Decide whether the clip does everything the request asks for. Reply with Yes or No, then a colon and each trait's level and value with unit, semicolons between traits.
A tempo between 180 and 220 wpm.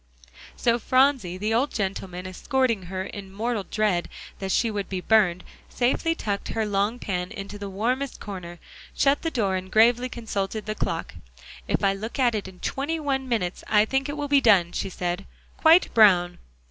Yes: average, 185 wpm